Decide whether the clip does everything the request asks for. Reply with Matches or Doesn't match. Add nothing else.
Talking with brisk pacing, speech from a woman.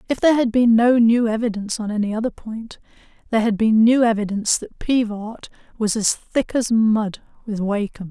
Doesn't match